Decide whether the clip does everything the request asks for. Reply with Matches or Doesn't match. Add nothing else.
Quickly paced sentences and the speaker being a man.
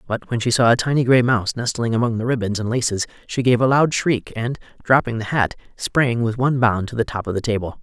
Matches